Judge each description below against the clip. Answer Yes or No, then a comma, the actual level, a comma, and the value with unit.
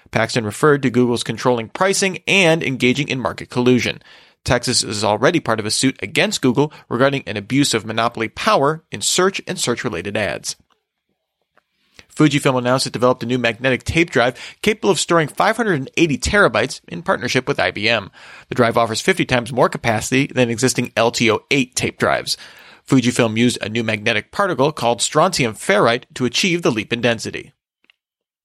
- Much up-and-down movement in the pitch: No, average, 4.1 semitones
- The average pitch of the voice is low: Yes, low, 125 Hz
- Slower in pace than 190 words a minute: Yes, average, 160 wpm